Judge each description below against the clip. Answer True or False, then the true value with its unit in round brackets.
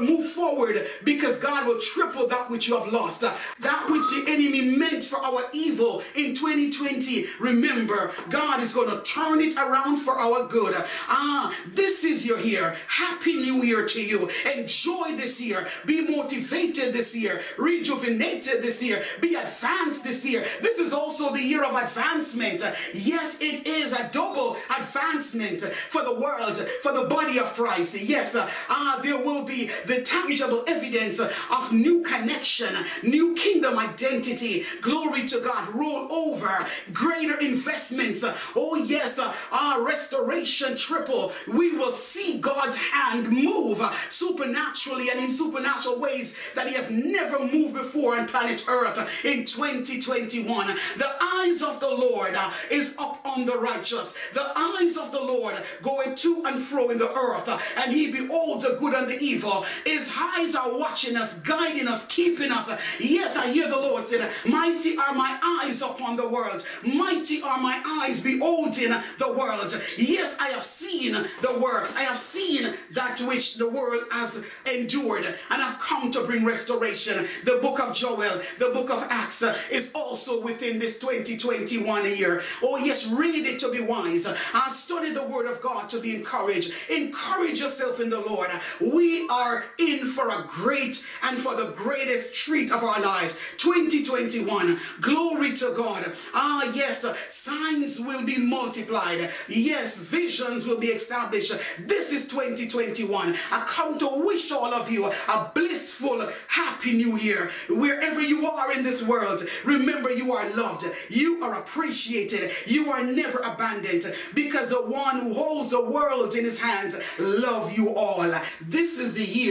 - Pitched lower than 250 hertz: False (265 Hz)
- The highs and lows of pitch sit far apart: False (4.4 semitones)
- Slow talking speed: False (160 wpm)